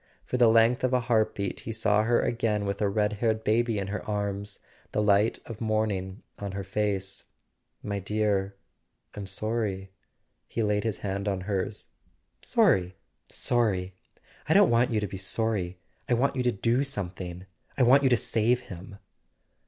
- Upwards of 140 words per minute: Yes, average, 170 wpm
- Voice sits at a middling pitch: No, low, 105 Hz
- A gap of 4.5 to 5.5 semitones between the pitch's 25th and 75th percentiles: No, average, 2.8 semitones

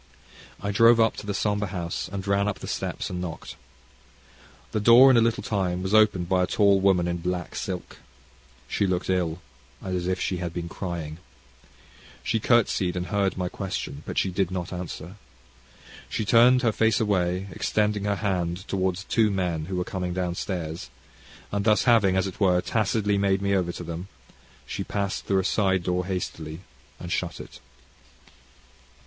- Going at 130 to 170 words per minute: No, average, 180 wpm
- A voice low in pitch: Yes, very low, 95 Hz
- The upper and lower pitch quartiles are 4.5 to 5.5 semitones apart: No, narrow, 2.4 semitones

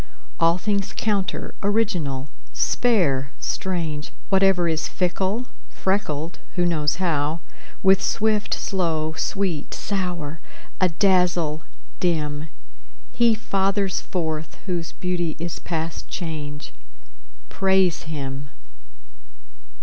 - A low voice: No, medium, 175 Hz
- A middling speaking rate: No, slow, 90 wpm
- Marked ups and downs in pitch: No, average, 3.6 semitones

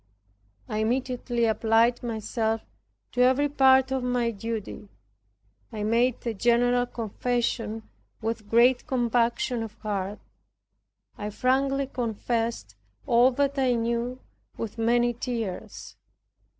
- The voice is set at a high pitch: Yes, high, 235 Hz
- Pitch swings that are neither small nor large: No, narrow, 2.0 semitones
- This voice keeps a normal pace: No, slow, 110 wpm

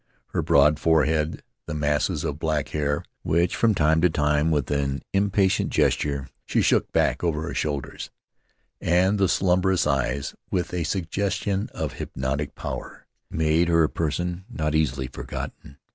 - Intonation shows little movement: No, average, 3.3 semitones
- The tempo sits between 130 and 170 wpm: Yes, average, 160 wpm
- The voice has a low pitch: Yes, very low, 80 Hz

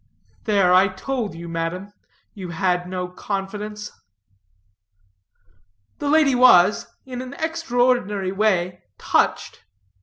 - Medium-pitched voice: No, high, 200 Hz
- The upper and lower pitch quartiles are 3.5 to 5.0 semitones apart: No, wide, 5.4 semitones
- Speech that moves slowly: Yes, slow, 100 wpm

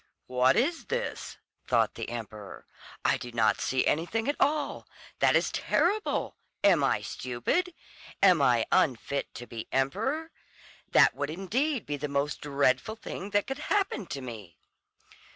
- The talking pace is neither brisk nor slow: Yes, average, 150 wpm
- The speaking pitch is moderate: Yes, medium, 150 Hz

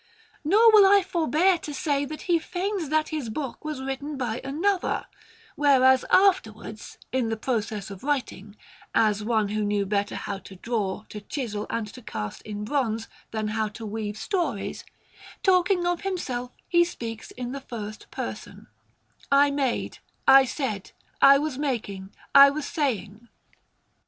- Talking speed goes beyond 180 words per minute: No, average, 155 wpm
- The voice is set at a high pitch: Yes, very high, 260 Hz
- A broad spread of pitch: Yes, wide, 6.1 semitones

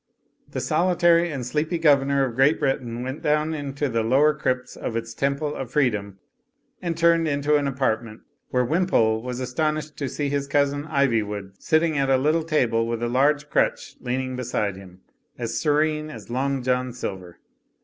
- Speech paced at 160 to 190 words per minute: Yes, average, 175 wpm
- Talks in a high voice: No, low, 135 Hz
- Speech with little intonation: No, average, 4.1 semitones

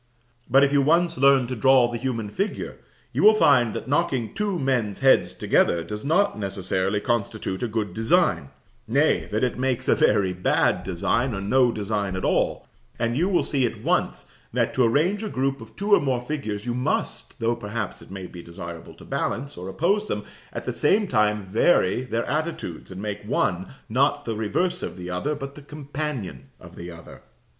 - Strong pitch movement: Yes, wide, 5.7 semitones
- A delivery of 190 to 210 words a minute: Yes, average, 195 wpm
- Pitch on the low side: Yes, low, 120 Hz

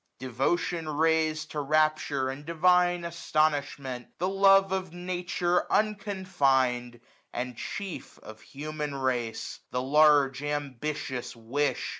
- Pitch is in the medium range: Yes, medium, 150 Hz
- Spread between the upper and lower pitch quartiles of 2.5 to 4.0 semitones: No, average, 4.8 semitones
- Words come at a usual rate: No, slow, 105 wpm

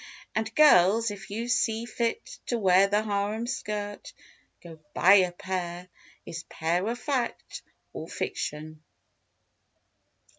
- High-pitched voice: Yes, high, 205 Hz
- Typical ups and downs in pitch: Yes, average, 4.2 semitones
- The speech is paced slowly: Yes, slow, 120 wpm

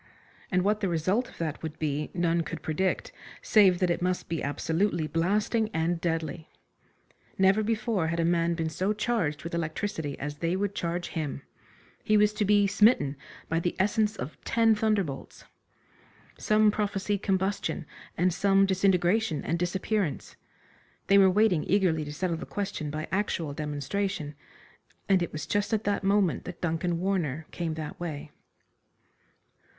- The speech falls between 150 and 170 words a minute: Yes, average, 155 wpm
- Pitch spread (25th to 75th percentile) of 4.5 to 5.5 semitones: No, average, 4.0 semitones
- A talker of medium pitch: Yes, medium, 180 Hz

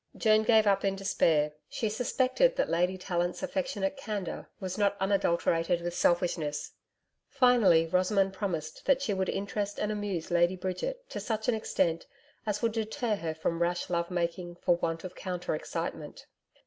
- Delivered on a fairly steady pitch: No, average, 3.9 semitones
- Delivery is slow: No, average, 160 wpm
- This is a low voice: No, high, 190 Hz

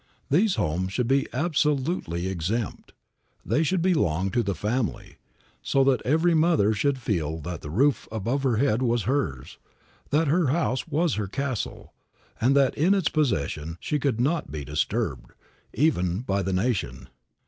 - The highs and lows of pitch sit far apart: Yes, wide, 7.7 semitones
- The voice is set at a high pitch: No, low, 125 Hz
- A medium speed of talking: Yes, average, 160 wpm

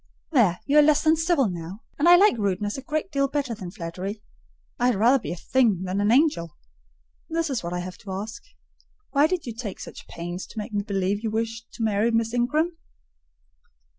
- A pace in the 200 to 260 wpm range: Yes, fast, 205 wpm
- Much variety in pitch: Yes, wide, 6.6 semitones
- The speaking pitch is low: No, high, 225 Hz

